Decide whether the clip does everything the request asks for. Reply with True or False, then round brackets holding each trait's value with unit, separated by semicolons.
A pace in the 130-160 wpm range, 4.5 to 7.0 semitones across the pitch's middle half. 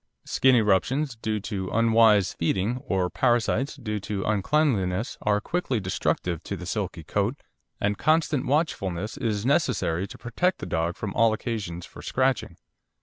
True (145 wpm; 5.2 semitones)